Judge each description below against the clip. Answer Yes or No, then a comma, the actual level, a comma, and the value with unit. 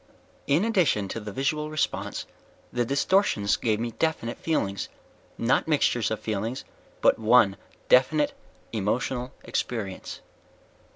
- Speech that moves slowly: Yes, slow, 120 wpm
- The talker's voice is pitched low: Yes, low, 125 Hz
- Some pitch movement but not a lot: No, wide, 6.0 semitones